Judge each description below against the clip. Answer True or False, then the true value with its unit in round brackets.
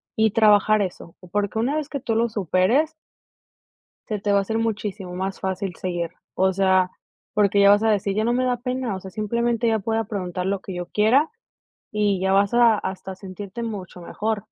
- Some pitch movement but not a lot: True (3.0 semitones)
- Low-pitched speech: False (205 Hz)